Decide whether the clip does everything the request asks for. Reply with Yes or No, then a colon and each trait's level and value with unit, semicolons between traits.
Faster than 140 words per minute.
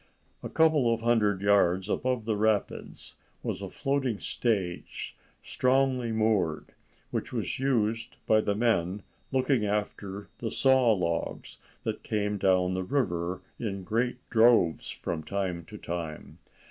No: slow, 135 wpm